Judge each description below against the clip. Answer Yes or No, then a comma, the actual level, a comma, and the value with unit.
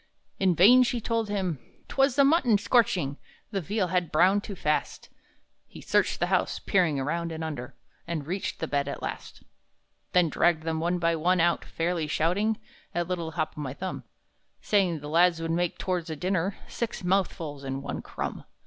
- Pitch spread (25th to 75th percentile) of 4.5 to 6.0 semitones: No, average, 3.5 semitones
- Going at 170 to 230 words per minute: Yes, average, 180 wpm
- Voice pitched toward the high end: No, medium, 175 Hz